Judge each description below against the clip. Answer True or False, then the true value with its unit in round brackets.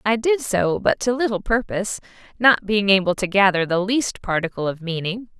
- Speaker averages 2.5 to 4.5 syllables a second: False (5.2 syllables/s)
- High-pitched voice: True (205 Hz)